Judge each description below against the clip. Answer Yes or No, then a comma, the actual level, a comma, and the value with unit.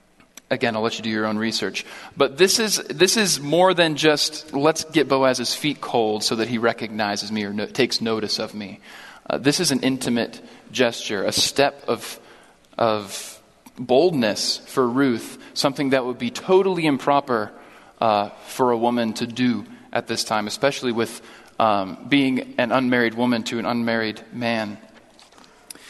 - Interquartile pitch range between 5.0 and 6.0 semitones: No, average, 4.2 semitones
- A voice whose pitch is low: Yes, low, 120 Hz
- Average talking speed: Yes, average, 165 wpm